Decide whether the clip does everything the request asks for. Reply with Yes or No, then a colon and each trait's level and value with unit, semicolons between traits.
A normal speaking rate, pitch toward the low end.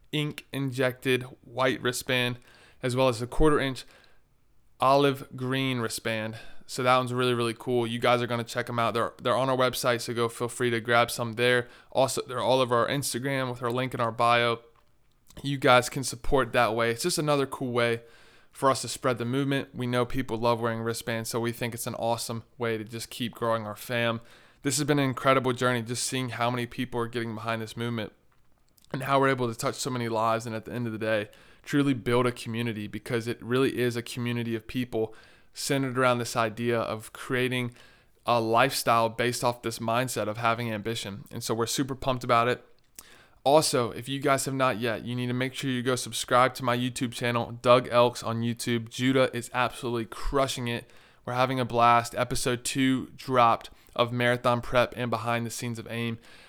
No: fast, 210 wpm; low, 120 Hz